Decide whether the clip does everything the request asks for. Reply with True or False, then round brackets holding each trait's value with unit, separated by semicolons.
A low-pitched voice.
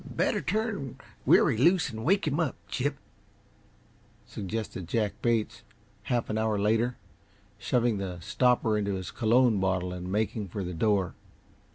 True (110 Hz)